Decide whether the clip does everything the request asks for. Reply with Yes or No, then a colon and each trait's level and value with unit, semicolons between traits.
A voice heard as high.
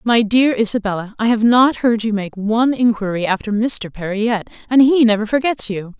Yes: high, 225 Hz